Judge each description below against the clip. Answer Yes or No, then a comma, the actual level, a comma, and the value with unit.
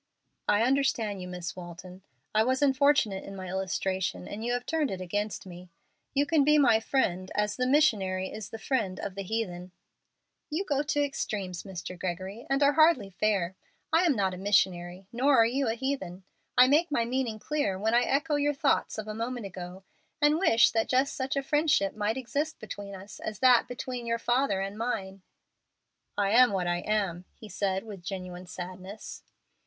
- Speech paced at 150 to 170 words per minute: No, average, 190 wpm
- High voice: Yes, high, 215 Hz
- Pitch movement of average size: No, wide, 5.9 semitones